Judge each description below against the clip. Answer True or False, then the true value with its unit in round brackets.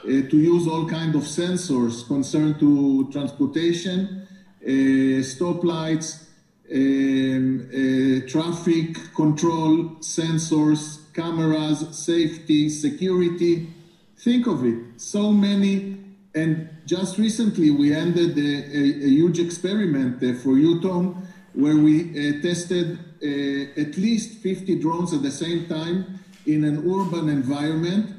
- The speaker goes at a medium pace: False (115 wpm)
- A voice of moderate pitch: True (160 Hz)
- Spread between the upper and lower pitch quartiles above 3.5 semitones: False (3.2 semitones)